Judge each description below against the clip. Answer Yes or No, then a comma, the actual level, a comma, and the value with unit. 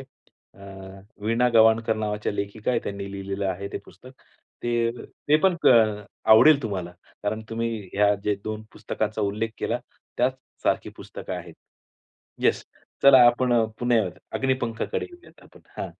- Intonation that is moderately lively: Yes, average, 3.3 semitones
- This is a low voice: Yes, low, 110 Hz